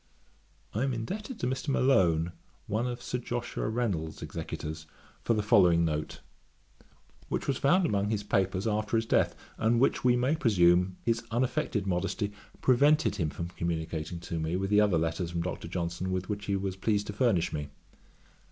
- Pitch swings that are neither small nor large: No, wide, 5.7 semitones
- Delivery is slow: No, average, 175 wpm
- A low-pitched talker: Yes, low, 100 Hz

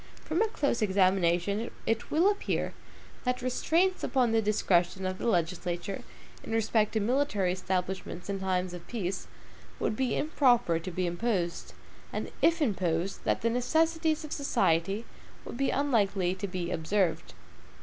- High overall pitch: Yes, high, 205 Hz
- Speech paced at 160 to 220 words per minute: No, average, 150 wpm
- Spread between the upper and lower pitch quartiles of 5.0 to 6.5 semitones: Yes, wide, 5.6 semitones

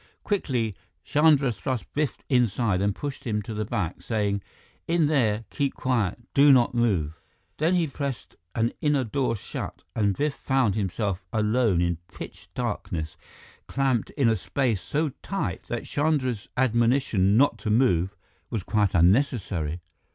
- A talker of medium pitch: No, low, 115 Hz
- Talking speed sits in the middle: Yes, average, 145 wpm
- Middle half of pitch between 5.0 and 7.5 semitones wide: Yes, average, 5.3 semitones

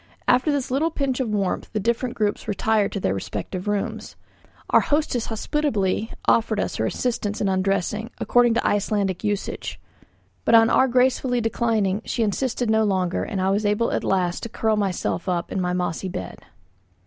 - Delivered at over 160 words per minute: Yes, average, 175 wpm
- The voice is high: Yes, high, 210 Hz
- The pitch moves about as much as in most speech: Yes, average, 3.7 semitones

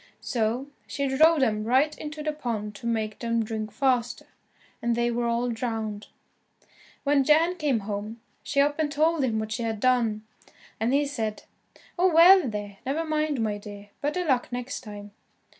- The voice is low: No, high, 240 Hz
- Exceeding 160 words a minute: Yes, average, 175 wpm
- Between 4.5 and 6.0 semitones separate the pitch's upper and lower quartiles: Yes, average, 5.1 semitones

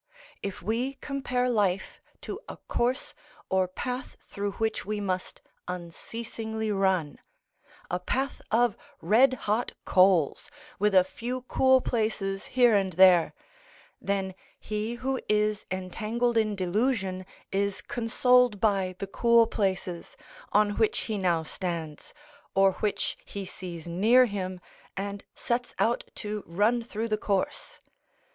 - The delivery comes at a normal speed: No, slow, 125 wpm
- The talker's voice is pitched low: No, high, 210 Hz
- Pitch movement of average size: Yes, average, 3.8 semitones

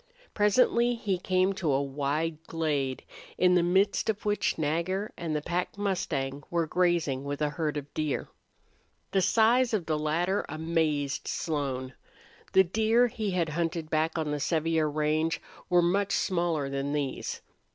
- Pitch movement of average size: Yes, average, 3.9 semitones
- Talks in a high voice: No, medium, 165 Hz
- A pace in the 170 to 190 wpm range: No, average, 155 wpm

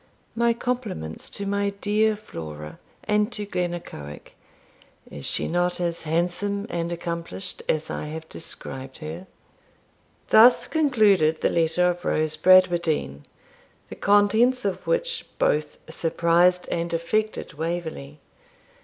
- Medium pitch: Yes, medium, 175 Hz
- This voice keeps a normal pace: No, slow, 120 wpm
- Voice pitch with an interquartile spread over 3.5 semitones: Yes, average, 4.3 semitones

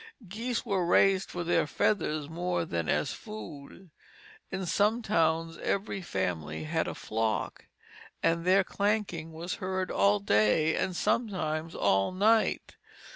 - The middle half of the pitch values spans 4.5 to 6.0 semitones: Yes, average, 5.3 semitones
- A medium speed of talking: No, slow, 130 wpm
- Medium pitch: Yes, medium, 170 Hz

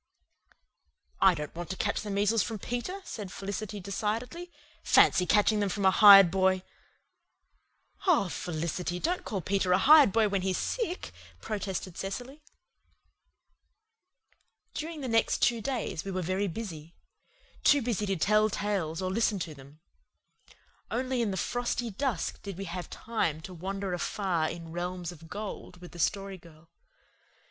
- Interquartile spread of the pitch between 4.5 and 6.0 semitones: No, average, 3.9 semitones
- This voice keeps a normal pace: Yes, average, 155 wpm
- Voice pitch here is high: Yes, high, 195 Hz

